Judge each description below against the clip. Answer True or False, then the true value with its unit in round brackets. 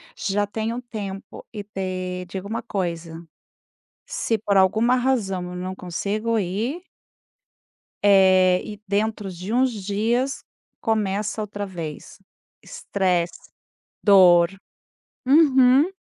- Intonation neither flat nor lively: True (3.4 semitones)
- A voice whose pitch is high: True (200 Hz)